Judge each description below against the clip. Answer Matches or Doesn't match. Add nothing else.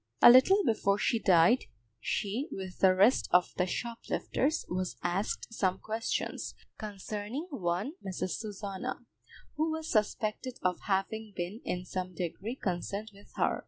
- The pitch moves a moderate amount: Matches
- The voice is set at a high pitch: Matches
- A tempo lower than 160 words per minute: Matches